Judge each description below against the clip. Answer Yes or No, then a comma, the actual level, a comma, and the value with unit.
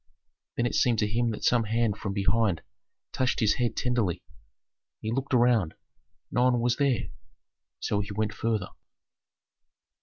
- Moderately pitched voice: No, low, 115 Hz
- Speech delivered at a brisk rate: No, average, 150 wpm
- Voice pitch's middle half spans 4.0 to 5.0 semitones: No, average, 2.8 semitones